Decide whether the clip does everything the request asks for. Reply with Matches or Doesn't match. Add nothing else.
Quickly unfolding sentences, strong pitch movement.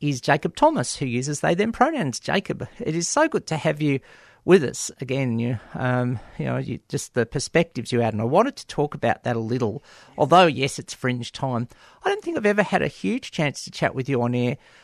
Matches